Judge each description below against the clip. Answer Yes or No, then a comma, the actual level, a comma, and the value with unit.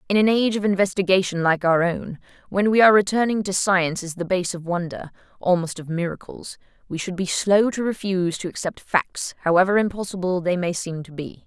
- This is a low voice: No, medium, 185 Hz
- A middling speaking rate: Yes, average, 190 wpm